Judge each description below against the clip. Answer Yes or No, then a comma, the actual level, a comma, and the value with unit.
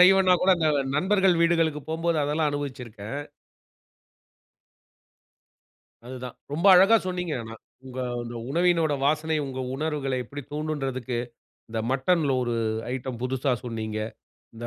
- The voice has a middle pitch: Yes, medium, 145 Hz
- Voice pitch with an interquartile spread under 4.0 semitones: No, average, 4.5 semitones